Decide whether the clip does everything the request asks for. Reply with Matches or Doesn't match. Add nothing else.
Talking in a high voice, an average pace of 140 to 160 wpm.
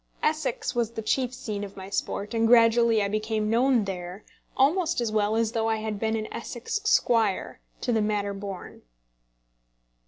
Doesn't match